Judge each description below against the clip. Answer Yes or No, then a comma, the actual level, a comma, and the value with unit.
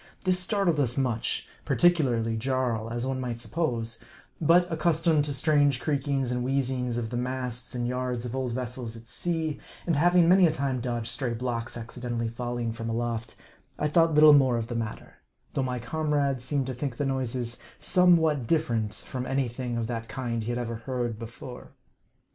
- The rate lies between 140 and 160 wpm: No, average, 185 wpm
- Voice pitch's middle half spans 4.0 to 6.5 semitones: No, average, 3.6 semitones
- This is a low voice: Yes, low, 125 Hz